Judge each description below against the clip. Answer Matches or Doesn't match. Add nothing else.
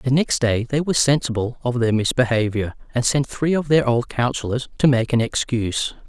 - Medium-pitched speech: Doesn't match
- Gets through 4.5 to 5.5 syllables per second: Matches